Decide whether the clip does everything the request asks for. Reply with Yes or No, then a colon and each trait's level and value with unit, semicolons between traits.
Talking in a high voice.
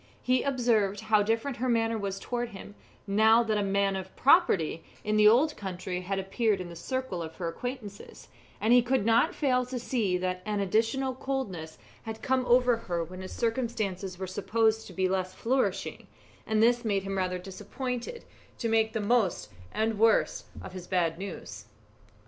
Yes: high, 215 Hz